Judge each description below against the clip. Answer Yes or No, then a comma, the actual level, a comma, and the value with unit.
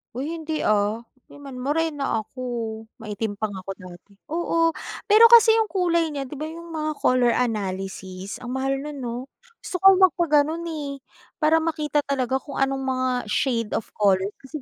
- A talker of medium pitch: No, very high, 275 Hz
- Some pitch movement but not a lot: No, wide, 6.0 semitones